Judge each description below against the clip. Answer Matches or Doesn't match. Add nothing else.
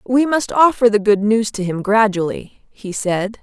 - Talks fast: Doesn't match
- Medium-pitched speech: Doesn't match